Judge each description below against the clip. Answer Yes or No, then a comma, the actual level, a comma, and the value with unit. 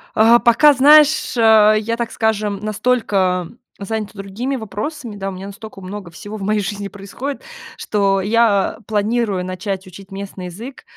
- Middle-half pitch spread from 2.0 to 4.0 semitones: Yes, average, 2.9 semitones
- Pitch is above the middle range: Yes, high, 210 Hz